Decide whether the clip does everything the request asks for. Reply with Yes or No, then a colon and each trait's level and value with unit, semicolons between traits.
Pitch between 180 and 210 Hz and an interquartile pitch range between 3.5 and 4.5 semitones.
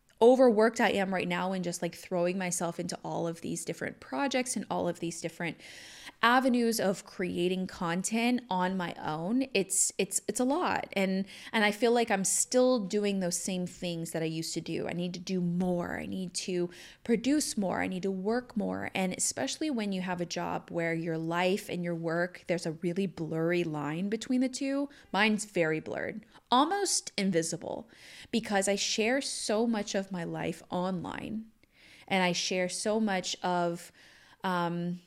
Yes: high, 190 Hz; average, 4.2 semitones